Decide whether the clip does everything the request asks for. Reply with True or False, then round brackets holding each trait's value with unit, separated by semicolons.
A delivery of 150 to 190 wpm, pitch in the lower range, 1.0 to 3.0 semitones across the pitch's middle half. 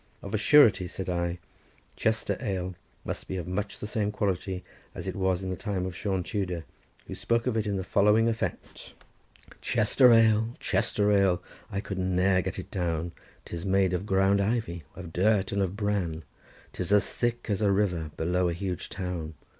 True (185 wpm; 95 Hz; 2.5 semitones)